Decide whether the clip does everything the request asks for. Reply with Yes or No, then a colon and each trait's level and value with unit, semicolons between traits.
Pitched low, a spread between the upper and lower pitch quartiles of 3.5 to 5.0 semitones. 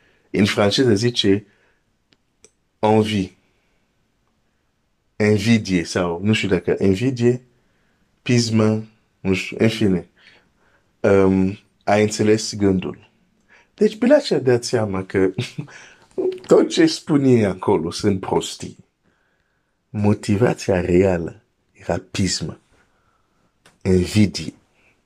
Yes: low, 105 Hz; average, 4.2 semitones